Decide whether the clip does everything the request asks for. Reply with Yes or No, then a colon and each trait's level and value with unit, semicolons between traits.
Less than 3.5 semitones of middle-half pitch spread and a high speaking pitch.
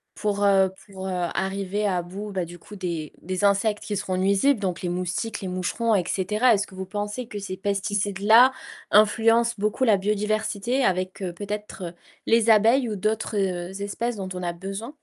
Yes: narrow, 2.4 semitones; high, 200 Hz